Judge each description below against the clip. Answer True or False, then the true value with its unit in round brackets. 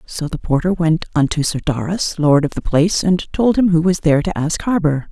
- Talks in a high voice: False (165 Hz)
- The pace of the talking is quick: True (235 wpm)